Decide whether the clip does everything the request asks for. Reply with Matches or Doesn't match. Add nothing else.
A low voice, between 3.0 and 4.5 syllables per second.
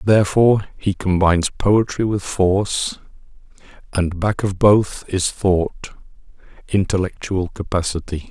Matches